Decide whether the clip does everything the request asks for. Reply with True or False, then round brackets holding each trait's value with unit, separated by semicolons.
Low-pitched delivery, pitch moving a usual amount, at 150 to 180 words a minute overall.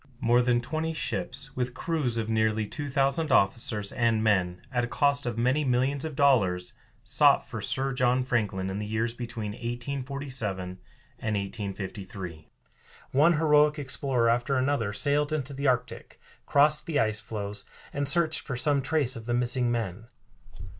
True (125 Hz; 4.4 semitones; 160 wpm)